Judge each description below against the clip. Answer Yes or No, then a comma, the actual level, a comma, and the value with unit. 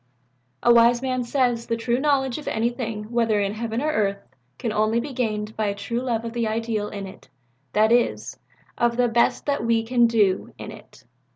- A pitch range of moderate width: No, narrow, 2.0 semitones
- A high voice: Yes, high, 230 Hz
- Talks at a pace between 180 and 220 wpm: Yes, average, 200 wpm